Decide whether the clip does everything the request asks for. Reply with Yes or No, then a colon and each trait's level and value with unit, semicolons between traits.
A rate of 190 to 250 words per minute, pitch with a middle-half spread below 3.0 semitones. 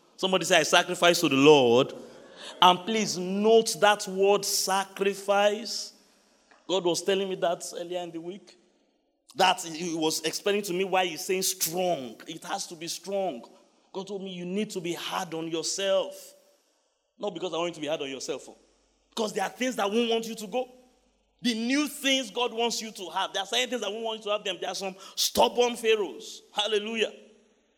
No: average, 200 wpm; average, 4.1 semitones